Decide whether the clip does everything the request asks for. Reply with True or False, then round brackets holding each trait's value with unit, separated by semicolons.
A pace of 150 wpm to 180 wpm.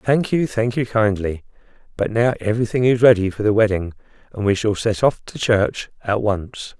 False (195 wpm)